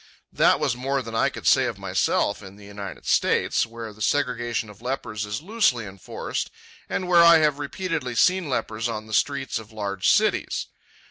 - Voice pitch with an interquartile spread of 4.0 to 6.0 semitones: Yes, average, 5.2 semitones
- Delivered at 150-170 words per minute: No, average, 185 wpm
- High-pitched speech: No, low, 120 Hz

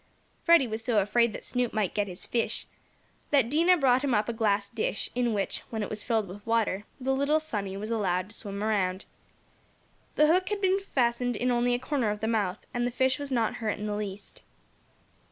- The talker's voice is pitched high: Yes, high, 230 Hz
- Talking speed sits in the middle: No, fast, 215 wpm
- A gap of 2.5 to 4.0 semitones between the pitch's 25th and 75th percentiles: Yes, average, 3.7 semitones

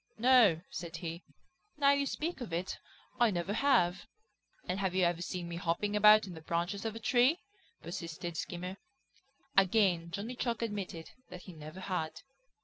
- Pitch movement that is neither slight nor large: Yes, average, 4.5 semitones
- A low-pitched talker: No, medium, 185 Hz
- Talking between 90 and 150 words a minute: No, average, 165 wpm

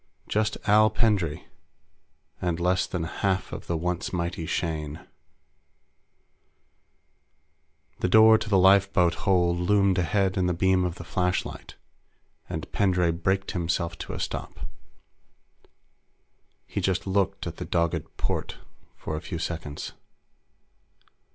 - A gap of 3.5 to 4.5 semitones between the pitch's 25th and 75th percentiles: No, narrow, 2.4 semitones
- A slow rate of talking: Yes, slow, 125 wpm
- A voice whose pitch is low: Yes, very low, 90 Hz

